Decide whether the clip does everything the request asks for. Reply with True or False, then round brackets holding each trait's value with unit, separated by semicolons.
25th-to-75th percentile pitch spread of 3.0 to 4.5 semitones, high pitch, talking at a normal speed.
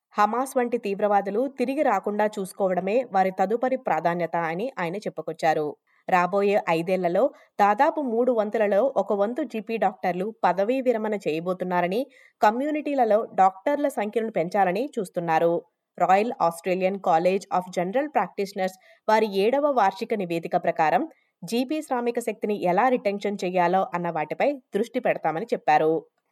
False (5.1 semitones; 205 Hz; 115 wpm)